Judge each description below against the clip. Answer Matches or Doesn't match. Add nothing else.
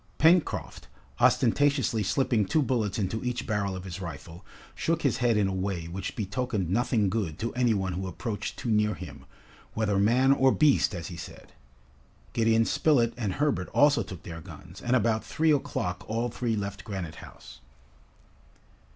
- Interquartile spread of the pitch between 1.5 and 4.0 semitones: Doesn't match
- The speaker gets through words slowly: Doesn't match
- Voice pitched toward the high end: Doesn't match